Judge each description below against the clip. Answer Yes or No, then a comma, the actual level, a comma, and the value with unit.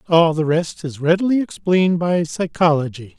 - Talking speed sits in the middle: Yes, average, 150 wpm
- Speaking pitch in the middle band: Yes, medium, 165 Hz